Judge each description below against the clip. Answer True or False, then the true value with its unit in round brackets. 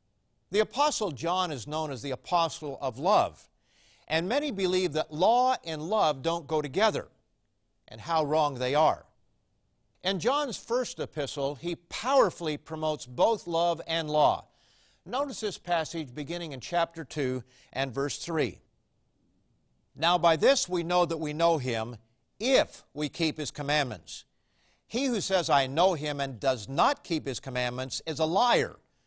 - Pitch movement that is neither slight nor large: True (4.3 semitones)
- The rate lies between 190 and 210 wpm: False (155 wpm)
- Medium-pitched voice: True (160 Hz)